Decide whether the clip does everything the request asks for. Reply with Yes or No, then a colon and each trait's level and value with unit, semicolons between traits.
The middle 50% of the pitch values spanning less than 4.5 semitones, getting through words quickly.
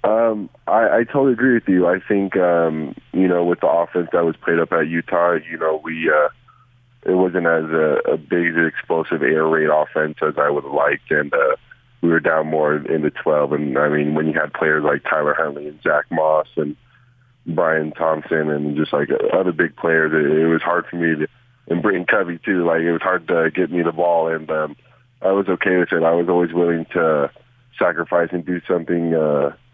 Yes: average, 2.8 semitones; fast, 220 wpm